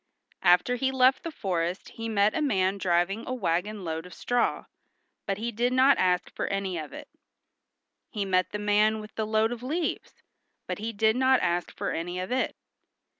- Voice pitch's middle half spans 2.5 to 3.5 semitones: No, average, 5.0 semitones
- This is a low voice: No, high, 210 Hz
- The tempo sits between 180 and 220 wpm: Yes, average, 190 wpm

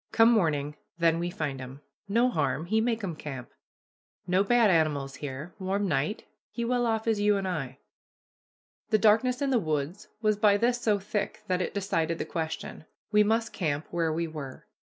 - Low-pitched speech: No, medium, 185 Hz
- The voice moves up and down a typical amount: No, wide, 5.9 semitones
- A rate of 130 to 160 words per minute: No, average, 185 wpm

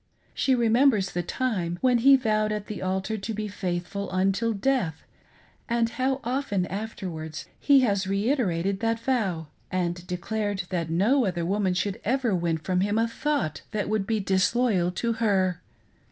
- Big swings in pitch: No, average, 4.0 semitones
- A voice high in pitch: Yes, high, 205 Hz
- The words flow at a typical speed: Yes, average, 160 wpm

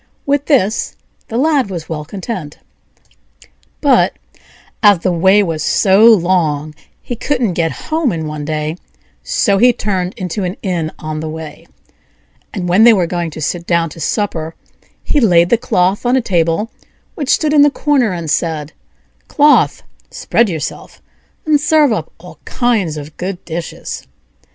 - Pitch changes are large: Yes, wide, 6.4 semitones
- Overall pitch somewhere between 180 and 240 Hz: Yes, medium, 185 Hz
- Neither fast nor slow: Yes, average, 160 wpm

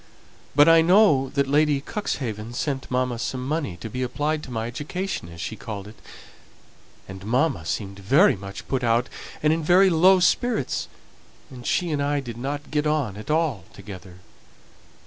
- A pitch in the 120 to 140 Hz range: Yes, low, 135 Hz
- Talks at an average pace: Yes, average, 165 wpm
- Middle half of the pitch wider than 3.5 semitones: Yes, wide, 5.6 semitones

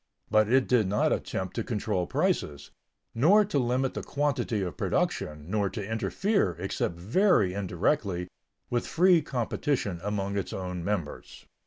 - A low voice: Yes, low, 105 Hz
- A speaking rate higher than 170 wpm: No, average, 145 wpm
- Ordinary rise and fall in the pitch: No, wide, 6.0 semitones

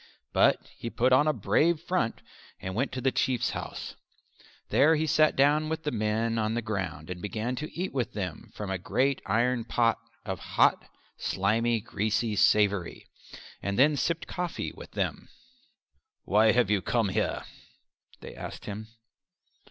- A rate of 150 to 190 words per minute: Yes, average, 160 wpm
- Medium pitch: No, low, 115 Hz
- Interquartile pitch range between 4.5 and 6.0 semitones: Yes, average, 4.8 semitones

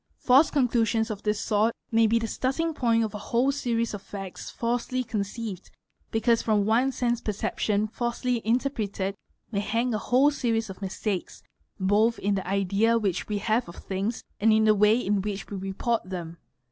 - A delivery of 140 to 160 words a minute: No, average, 185 wpm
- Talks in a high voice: Yes, high, 220 Hz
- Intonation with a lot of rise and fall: No, average, 2.8 semitones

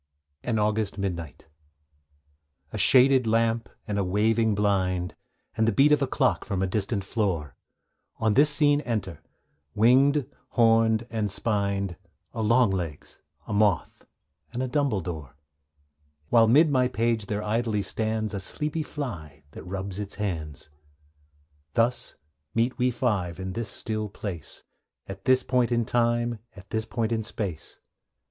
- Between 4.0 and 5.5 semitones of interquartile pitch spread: No, average, 3.5 semitones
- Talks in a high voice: No, low, 110 Hz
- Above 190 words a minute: No, average, 140 wpm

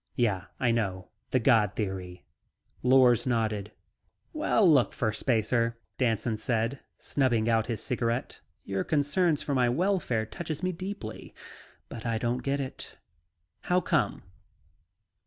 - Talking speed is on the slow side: Yes, slow, 125 wpm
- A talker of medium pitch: No, low, 120 Hz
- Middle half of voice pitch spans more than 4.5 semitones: No, average, 4.0 semitones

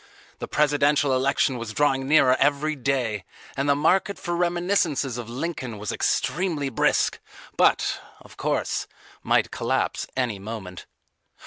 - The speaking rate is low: Yes, slow, 130 wpm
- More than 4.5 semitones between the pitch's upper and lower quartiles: No, average, 3.9 semitones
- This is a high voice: No, medium, 140 Hz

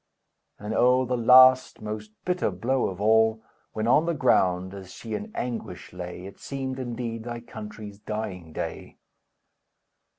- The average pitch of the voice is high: No, low, 110 Hz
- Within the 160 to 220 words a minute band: No, average, 145 wpm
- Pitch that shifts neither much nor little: Yes, average, 3.8 semitones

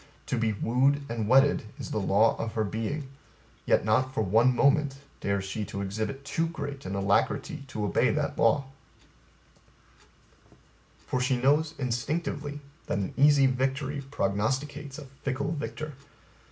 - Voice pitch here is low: Yes, low, 130 Hz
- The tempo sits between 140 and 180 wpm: Yes, average, 145 wpm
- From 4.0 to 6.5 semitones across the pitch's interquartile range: Yes, average, 4.6 semitones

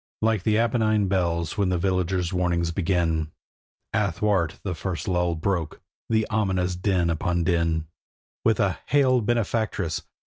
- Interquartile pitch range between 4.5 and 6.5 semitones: No, average, 3.8 semitones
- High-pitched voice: No, very low, 90 Hz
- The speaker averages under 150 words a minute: Yes, slow, 135 wpm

